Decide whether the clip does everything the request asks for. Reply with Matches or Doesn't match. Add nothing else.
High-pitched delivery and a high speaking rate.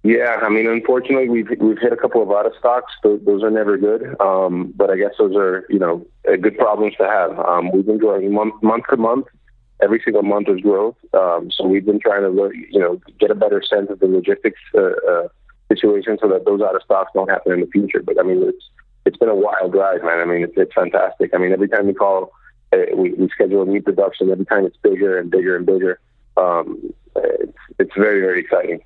Matches